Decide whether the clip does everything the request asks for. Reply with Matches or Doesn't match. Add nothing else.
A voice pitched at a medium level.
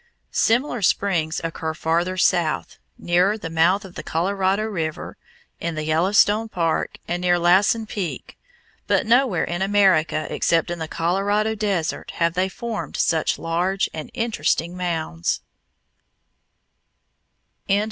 Matches